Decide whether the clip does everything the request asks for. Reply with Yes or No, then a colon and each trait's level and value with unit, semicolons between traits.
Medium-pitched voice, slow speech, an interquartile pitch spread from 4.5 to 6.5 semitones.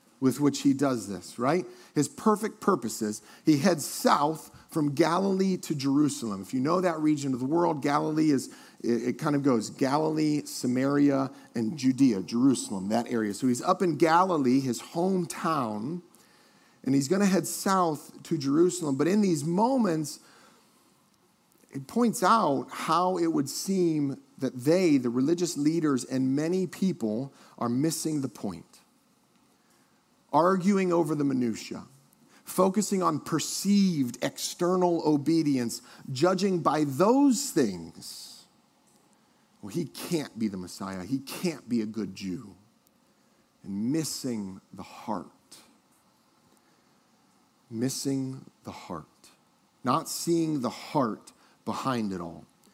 Yes: medium, 150 Hz; slow, 130 wpm; average, 5.3 semitones